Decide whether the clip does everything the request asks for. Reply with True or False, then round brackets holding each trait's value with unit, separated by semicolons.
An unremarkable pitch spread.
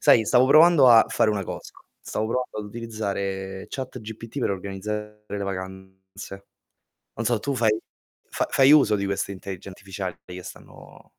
True (3.3 semitones)